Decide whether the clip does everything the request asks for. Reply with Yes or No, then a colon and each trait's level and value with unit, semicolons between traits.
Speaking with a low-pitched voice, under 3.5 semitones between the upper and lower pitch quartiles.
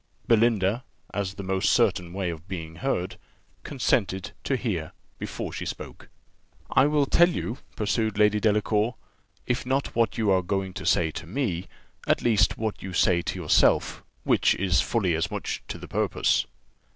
No: low, 100 Hz; average, 4.3 semitones